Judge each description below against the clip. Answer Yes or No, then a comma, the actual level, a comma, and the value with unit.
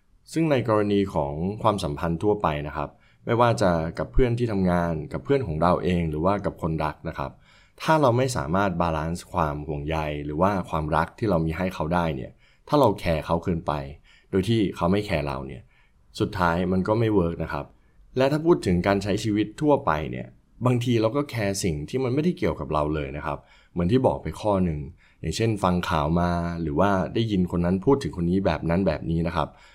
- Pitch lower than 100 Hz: Yes, very low, 90 Hz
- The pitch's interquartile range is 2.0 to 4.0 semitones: No, average, 5.2 semitones